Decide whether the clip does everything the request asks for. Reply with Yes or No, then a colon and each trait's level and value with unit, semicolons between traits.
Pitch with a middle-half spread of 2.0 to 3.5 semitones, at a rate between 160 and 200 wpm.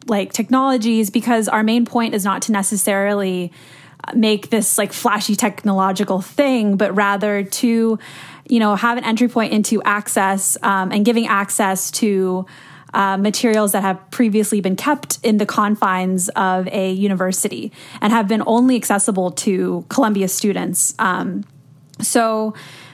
No: average, 2.9 semitones; average, 145 wpm